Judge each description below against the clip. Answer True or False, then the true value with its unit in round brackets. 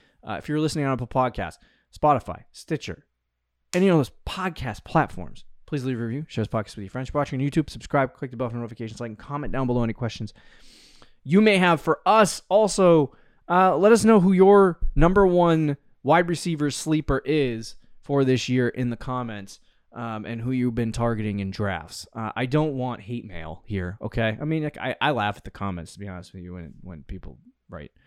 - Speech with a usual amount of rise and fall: False (6.0 semitones)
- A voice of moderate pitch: False (125 Hz)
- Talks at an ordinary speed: False (215 wpm)